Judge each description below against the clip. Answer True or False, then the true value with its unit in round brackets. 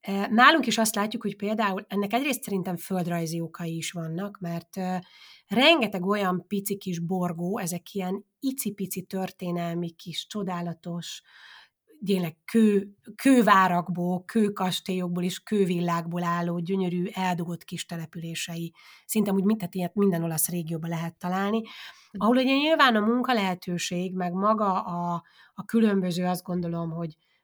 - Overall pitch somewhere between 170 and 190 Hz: True (185 Hz)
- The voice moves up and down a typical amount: True (3.0 semitones)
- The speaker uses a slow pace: False (125 wpm)